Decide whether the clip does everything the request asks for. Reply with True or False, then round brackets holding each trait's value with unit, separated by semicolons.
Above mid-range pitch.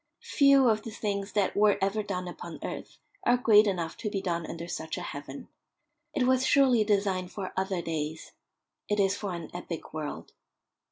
True (195 Hz)